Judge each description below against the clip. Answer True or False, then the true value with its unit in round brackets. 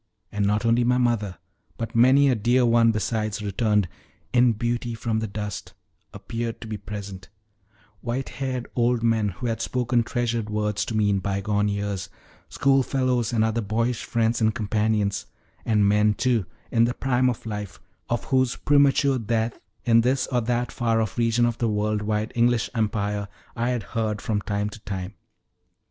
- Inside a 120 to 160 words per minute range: False (170 wpm)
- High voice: False (115 Hz)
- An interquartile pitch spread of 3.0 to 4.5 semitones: False (2.4 semitones)